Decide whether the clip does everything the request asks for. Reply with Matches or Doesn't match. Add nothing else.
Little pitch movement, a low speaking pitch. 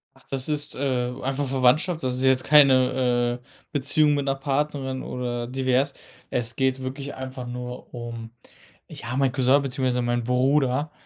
Matches